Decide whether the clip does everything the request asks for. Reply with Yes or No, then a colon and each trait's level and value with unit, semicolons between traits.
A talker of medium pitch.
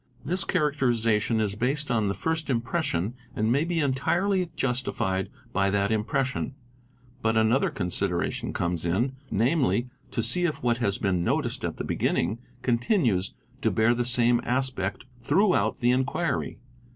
No: low, 120 Hz